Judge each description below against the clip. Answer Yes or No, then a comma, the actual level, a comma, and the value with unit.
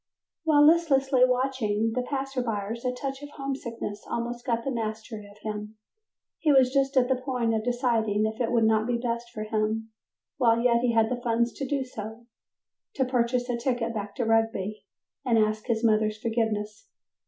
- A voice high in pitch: Yes, high, 235 Hz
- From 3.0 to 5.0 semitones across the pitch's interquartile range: No, narrow, 2.6 semitones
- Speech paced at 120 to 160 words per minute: No, average, 180 wpm